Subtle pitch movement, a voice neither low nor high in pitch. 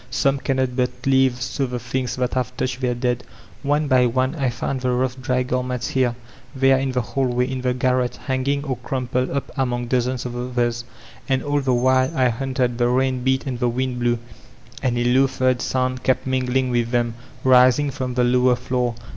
No: narrow, 1.1 semitones; low, 125 Hz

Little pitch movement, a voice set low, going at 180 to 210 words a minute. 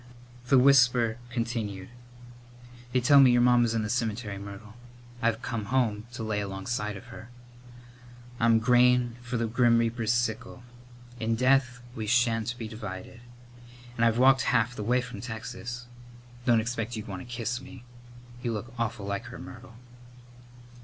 No: narrow, 2.0 semitones; low, 115 Hz; average, 155 wpm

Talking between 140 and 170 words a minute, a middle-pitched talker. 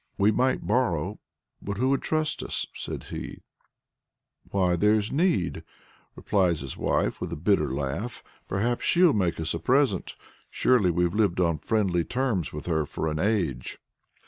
No: average, 155 wpm; very low, 95 Hz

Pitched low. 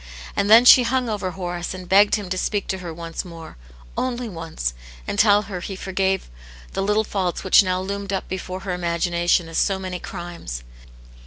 No: high, 190 Hz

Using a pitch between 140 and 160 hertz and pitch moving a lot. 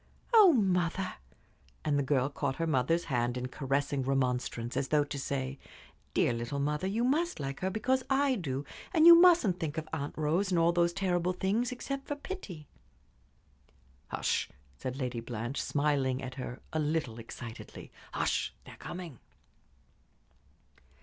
Yes: medium, 150 Hz; wide, 6.3 semitones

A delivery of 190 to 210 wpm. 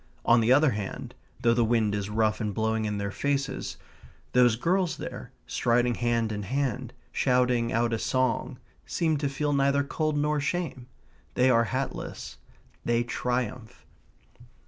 No: average, 150 wpm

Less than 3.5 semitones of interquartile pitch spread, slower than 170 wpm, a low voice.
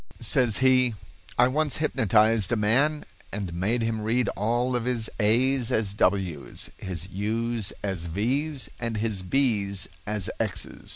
No: average, 3.8 semitones; average, 140 wpm; low, 115 Hz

